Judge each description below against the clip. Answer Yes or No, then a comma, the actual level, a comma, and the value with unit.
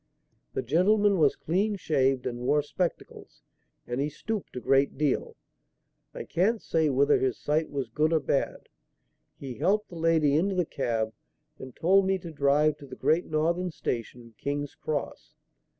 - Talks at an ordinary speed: Yes, average, 165 wpm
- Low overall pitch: No, medium, 150 Hz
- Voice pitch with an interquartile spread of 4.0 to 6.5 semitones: Yes, average, 4.4 semitones